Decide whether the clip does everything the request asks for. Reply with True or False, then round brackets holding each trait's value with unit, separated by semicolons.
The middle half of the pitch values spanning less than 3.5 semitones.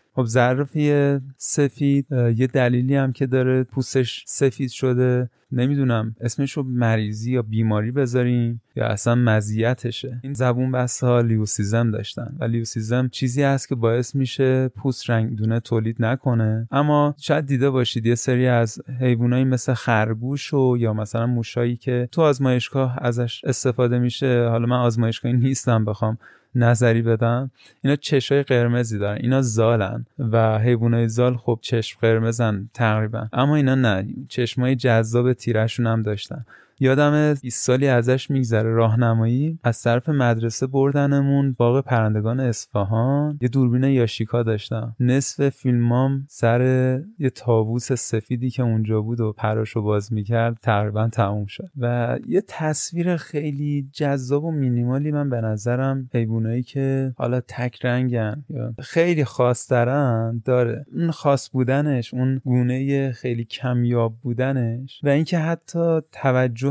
True (2.6 semitones)